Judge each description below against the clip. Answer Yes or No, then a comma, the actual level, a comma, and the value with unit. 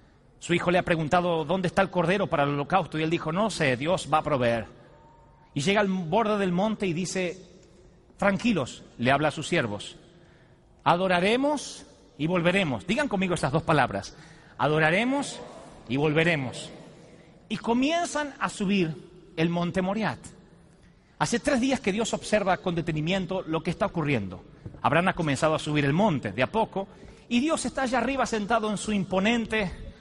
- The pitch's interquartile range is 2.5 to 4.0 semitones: No, average, 4.7 semitones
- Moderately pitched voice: Yes, medium, 180 Hz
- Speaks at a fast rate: No, average, 170 wpm